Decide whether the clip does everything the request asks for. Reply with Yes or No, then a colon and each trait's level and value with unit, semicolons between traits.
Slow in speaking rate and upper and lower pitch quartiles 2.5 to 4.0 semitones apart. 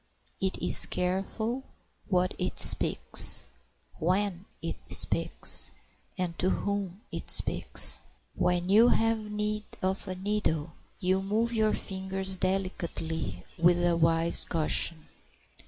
Yes: slow, 115 wpm; average, 2.9 semitones